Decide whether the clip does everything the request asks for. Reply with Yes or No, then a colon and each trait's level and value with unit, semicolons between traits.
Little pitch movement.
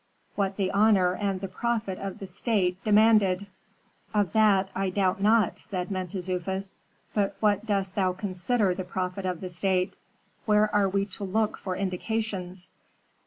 Yes: narrow, 2.2 semitones